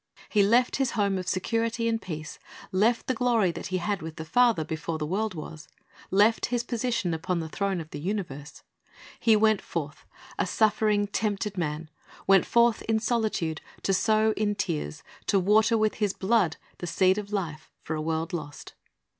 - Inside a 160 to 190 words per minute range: Yes, average, 180 wpm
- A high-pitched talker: Yes, high, 200 Hz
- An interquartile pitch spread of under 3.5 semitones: No, average, 5.0 semitones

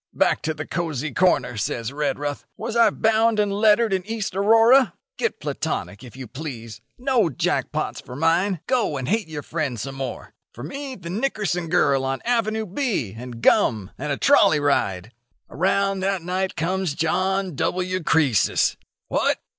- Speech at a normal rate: Yes, average, 165 wpm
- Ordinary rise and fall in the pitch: No, wide, 7.2 semitones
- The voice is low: No, medium, 175 Hz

